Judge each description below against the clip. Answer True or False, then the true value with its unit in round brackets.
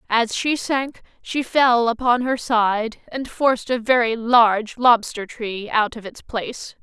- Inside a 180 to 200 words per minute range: False (165 wpm)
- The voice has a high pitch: True (235 Hz)